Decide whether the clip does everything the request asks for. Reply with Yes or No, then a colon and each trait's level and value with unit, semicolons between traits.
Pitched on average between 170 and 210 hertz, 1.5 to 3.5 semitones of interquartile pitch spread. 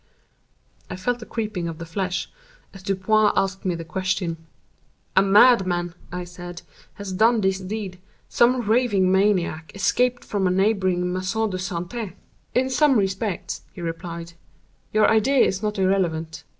Yes: high, 190 Hz; average, 3.2 semitones